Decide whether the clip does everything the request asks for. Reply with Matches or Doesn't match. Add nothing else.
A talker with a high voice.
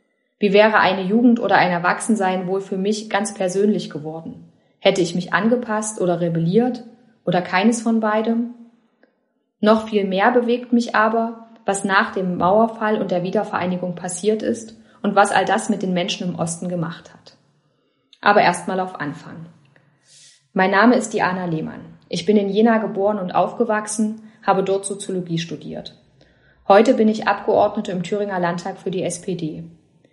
Matches